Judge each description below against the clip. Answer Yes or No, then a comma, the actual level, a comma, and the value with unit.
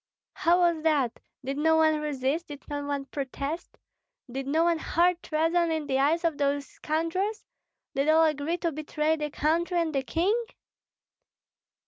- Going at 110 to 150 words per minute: No, average, 160 wpm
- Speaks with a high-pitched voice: Yes, very high, 310 Hz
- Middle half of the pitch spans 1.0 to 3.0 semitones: Yes, narrow, 2.6 semitones